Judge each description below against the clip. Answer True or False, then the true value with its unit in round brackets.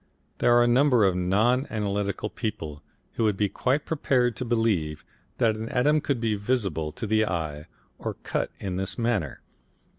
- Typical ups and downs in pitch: True (4.2 semitones)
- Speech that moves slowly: False (175 wpm)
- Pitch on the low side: True (110 Hz)